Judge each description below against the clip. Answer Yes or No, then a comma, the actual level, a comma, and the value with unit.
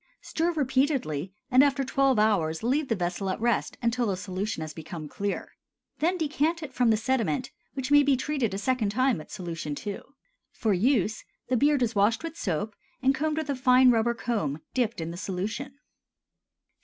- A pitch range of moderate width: No, wide, 5.8 semitones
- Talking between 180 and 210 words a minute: Yes, average, 185 wpm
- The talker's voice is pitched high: Yes, high, 235 Hz